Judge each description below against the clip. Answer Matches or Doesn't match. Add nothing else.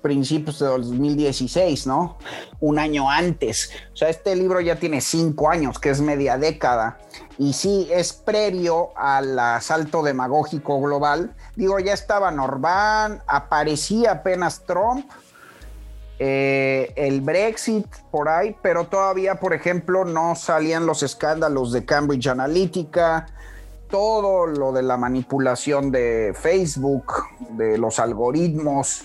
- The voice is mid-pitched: Matches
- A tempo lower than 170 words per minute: Matches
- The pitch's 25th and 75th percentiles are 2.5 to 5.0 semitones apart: Matches